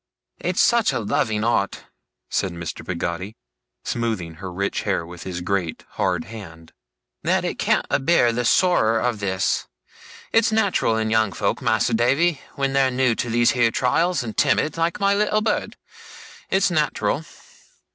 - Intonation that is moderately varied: No, wide, 6.3 semitones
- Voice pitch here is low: Yes, low, 115 Hz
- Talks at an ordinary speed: Yes, average, 155 wpm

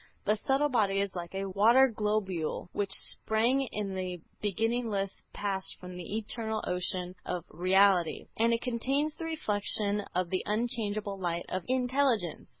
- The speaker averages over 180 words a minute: No, average, 150 wpm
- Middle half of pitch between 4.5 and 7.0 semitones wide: No, average, 3.7 semitones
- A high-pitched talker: Yes, high, 205 Hz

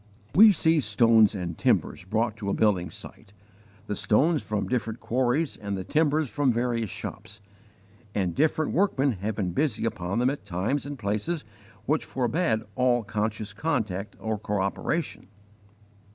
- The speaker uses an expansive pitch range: Yes, wide, 5.7 semitones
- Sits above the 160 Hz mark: No, low, 110 Hz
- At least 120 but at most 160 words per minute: Yes, average, 150 wpm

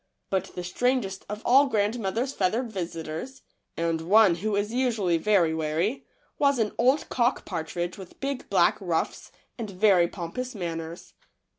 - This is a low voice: No, high, 200 Hz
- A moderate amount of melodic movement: No, wide, 5.7 semitones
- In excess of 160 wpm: No, average, 155 wpm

